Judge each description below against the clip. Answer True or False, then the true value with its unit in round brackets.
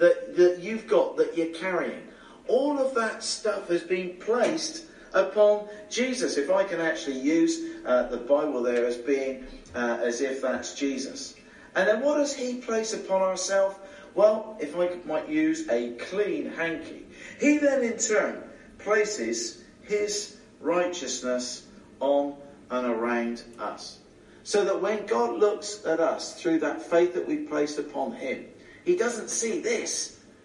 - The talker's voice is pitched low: False (195 Hz)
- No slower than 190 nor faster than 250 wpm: False (155 wpm)